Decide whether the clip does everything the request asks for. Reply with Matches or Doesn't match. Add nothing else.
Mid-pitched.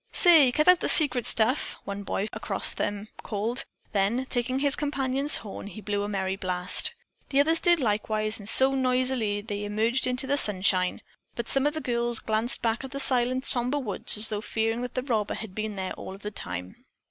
Doesn't match